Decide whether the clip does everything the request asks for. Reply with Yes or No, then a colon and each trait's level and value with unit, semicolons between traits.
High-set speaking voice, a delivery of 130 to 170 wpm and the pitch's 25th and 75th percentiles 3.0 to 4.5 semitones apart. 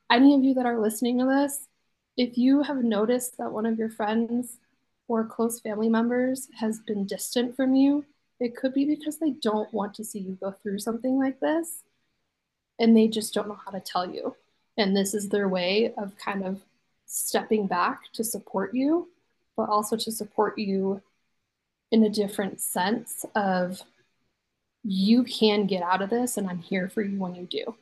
No: high, 220 Hz; average, 190 wpm; average, 3.3 semitones